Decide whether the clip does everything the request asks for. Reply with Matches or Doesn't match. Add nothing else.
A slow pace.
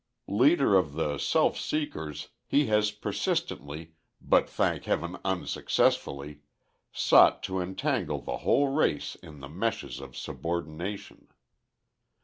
Matches